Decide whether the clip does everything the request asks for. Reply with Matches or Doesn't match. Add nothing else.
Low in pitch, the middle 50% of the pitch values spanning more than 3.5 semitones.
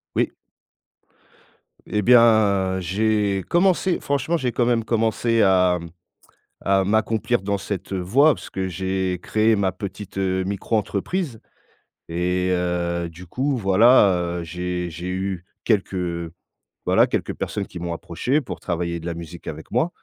Matches